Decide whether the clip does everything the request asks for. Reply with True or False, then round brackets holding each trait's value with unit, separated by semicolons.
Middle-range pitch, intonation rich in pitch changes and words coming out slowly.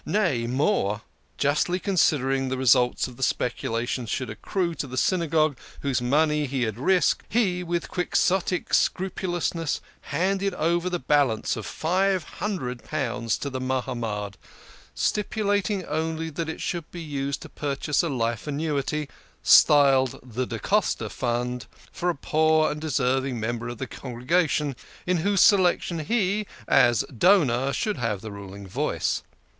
False (145 Hz; 6.0 semitones; 145 wpm)